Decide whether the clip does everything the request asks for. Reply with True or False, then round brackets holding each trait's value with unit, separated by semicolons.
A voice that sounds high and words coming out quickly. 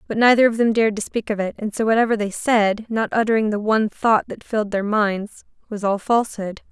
True (215 Hz; 215 wpm)